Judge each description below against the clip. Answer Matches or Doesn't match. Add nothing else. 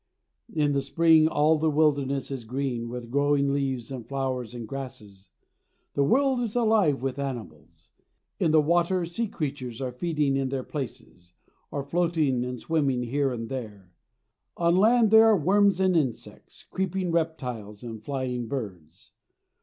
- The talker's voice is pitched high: Doesn't match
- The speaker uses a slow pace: Doesn't match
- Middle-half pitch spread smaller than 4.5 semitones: Doesn't match